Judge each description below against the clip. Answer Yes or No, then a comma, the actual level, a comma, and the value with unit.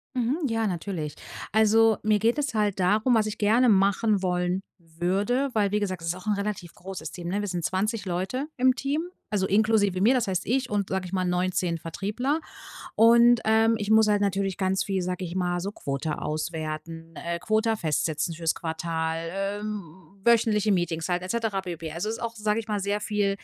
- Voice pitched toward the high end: Yes, high, 195 Hz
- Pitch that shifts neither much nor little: Yes, average, 3.7 semitones